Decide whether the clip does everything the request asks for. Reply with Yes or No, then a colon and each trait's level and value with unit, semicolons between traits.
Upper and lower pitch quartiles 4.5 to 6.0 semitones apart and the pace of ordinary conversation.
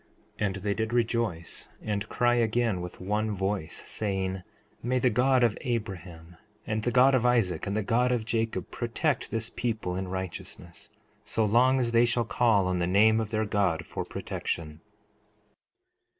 No: average, 3.9 semitones; average, 170 wpm